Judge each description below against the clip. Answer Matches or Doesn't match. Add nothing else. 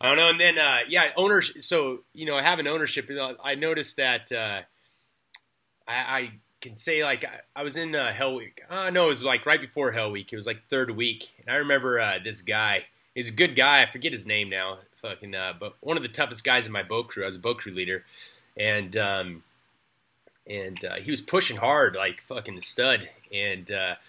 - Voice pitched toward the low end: Matches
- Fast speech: Matches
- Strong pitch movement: Matches